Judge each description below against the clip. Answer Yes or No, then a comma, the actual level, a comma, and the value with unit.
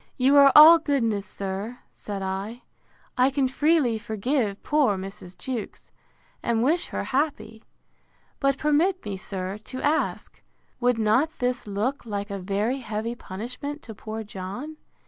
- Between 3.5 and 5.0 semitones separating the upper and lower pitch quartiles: No, wide, 5.5 semitones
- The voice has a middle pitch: No, high, 235 Hz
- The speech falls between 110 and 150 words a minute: Yes, average, 145 wpm